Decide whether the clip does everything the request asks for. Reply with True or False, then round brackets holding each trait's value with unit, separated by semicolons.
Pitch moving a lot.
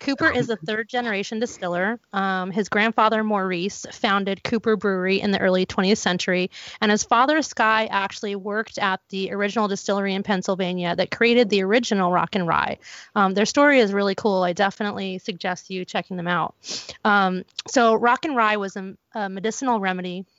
False (2.7 semitones)